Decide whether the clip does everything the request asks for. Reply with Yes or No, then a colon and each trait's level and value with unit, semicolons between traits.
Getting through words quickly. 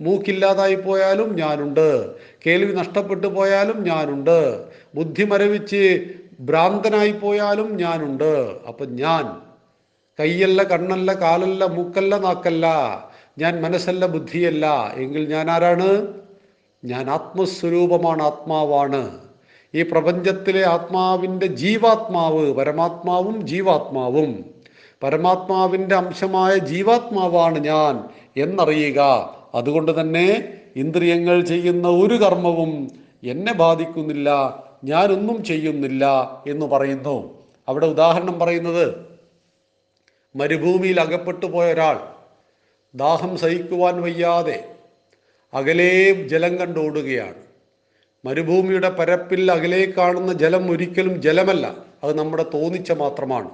No: average, 80 wpm